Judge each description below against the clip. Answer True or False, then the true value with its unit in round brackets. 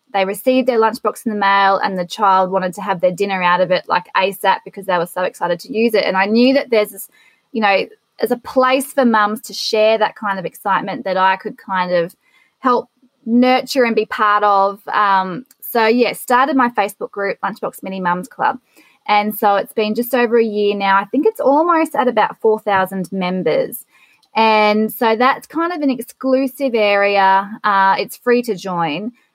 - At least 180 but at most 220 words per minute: True (200 wpm)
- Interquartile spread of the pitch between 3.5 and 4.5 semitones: True (4.1 semitones)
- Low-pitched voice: False (215 Hz)